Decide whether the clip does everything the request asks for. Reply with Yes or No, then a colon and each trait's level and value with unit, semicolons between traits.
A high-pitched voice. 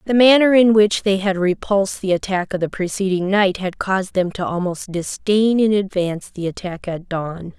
Yes: high, 195 Hz